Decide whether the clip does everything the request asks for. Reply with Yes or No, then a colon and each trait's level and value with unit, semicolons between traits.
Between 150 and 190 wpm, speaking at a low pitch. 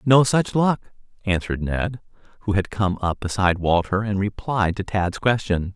Yes: average, 165 wpm; low, 100 Hz